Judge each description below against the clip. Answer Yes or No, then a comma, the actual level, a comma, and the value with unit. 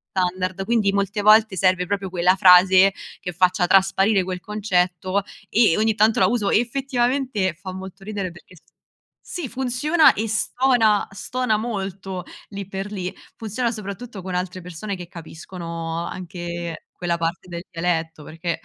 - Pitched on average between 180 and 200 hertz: Yes, high, 190 Hz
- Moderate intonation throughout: Yes, average, 3.3 semitones